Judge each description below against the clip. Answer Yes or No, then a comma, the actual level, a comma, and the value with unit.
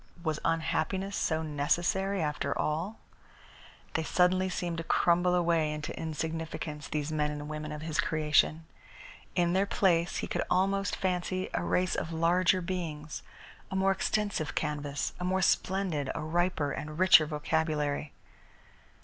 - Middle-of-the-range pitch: Yes, medium, 165 Hz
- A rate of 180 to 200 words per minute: No, average, 140 wpm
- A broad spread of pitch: No, average, 3.2 semitones